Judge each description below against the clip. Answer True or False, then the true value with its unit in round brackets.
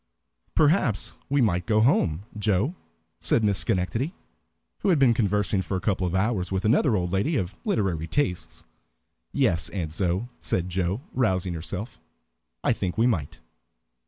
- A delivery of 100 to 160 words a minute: True (155 wpm)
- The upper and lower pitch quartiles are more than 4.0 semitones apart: True (4.4 semitones)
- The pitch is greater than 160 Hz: False (100 Hz)